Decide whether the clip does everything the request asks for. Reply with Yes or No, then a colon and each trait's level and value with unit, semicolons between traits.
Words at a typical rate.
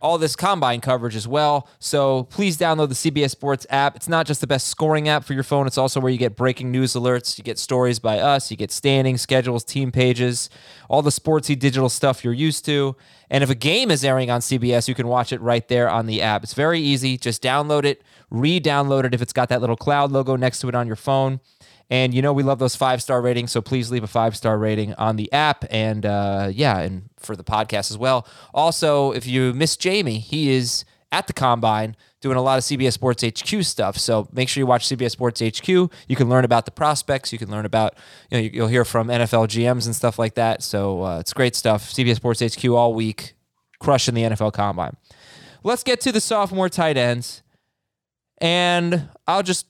No: fast, 225 wpm